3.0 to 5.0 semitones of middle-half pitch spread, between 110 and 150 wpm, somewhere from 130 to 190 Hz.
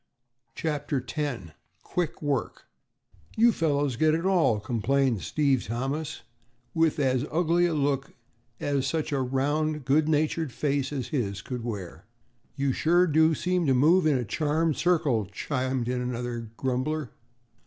Yes: average, 3.9 semitones; average, 145 wpm; medium, 140 Hz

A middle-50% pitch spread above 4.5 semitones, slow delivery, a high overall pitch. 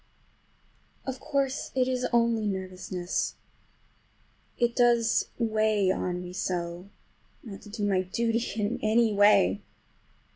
No: average, 4.1 semitones; slow, 115 wpm; high, 215 Hz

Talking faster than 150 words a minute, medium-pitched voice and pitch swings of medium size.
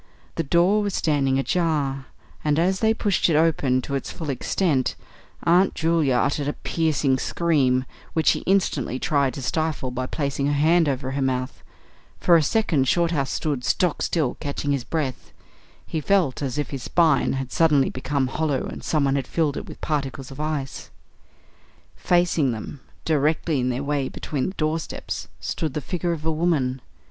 Yes: average, 175 wpm; medium, 145 Hz; average, 3.5 semitones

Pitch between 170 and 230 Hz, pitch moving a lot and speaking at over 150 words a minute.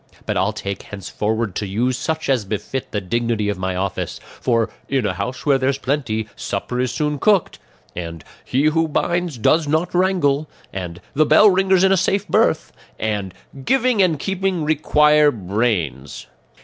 No: low, 130 Hz; wide, 7.4 semitones; average, 170 wpm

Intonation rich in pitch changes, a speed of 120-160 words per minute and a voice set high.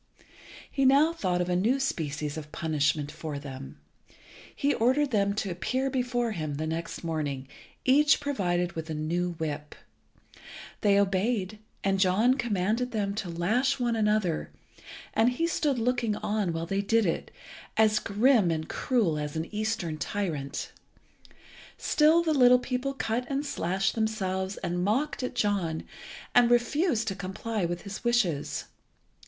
Yes: wide, 6.4 semitones; average, 150 wpm; high, 205 Hz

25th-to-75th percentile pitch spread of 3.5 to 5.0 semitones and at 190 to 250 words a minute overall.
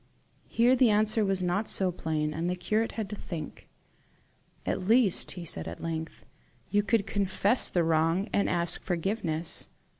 No: average, 4.2 semitones; average, 160 wpm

